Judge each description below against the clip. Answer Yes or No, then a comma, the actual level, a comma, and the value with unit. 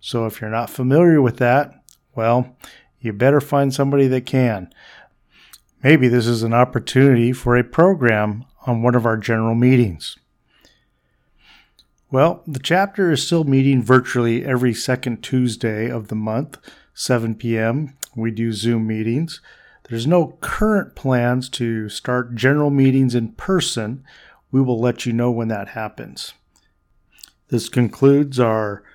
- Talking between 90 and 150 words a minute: Yes, average, 140 wpm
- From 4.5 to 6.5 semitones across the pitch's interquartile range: No, average, 3.0 semitones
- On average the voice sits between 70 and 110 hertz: No, low, 125 Hz